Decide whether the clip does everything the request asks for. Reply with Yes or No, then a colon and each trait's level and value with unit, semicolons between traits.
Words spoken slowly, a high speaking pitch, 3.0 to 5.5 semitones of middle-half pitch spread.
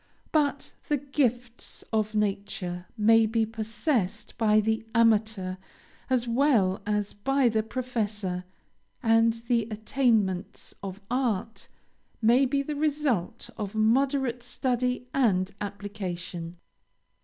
Yes: slow, 110 wpm; high, 225 Hz; average, 3.6 semitones